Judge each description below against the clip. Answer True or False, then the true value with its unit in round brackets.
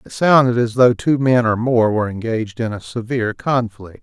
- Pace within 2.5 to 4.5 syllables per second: False (5.4 syllables/s)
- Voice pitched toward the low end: True (115 Hz)